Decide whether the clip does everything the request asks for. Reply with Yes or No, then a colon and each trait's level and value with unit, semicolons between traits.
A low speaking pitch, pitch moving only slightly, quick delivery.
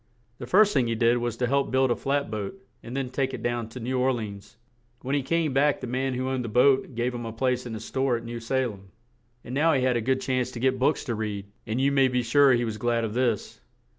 Yes: low, 125 Hz; narrow, 2.3 semitones; fast, 280 wpm